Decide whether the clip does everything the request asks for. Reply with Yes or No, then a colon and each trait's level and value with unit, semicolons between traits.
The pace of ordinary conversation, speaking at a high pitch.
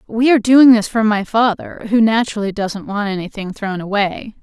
Yes: average, 190 wpm; high, 215 Hz